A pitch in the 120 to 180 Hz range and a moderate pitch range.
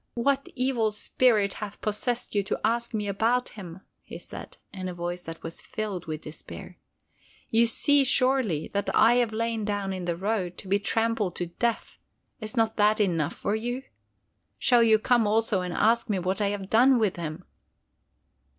No: high, 215 Hz; average, 3.8 semitones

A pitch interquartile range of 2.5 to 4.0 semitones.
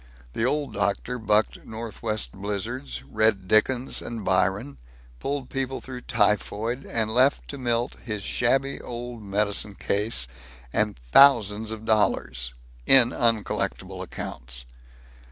Yes: average, 3.3 semitones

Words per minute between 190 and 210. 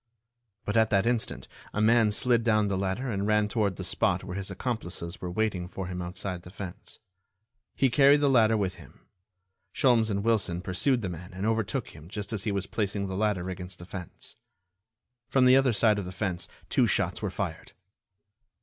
Yes: average, 195 wpm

